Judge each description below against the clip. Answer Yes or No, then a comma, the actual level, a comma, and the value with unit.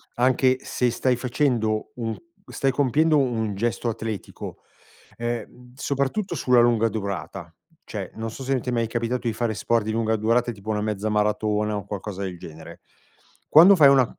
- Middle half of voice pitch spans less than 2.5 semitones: No, average, 2.9 semitones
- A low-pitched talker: Yes, low, 115 Hz